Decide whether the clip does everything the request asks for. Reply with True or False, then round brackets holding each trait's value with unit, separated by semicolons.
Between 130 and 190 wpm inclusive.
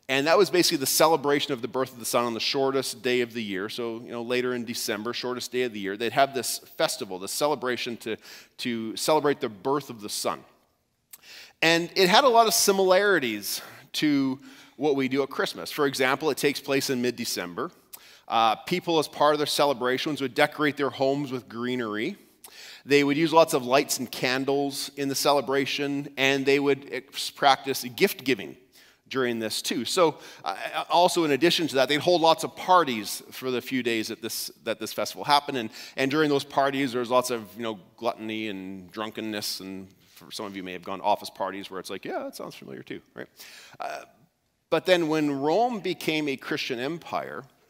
False (205 wpm)